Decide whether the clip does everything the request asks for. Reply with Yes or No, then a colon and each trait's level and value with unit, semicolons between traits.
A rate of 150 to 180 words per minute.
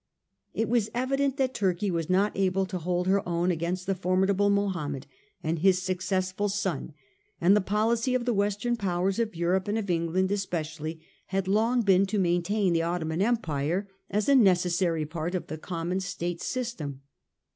Yes: average, 170 wpm